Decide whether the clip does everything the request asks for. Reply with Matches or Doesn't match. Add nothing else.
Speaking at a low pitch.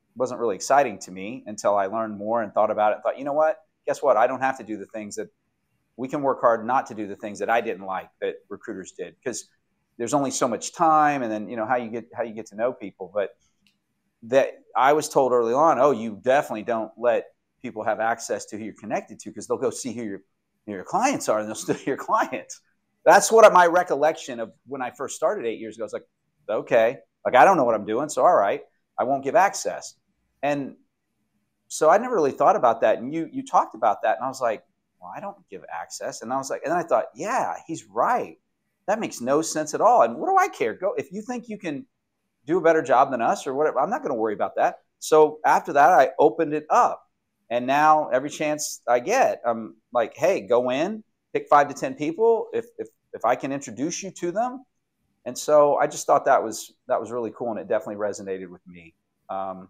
Doesn't match